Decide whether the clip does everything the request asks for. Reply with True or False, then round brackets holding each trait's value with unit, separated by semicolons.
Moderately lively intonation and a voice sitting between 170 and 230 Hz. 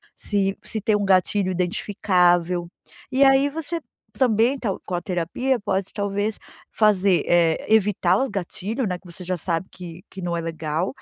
True (3.5 semitones; 190 Hz)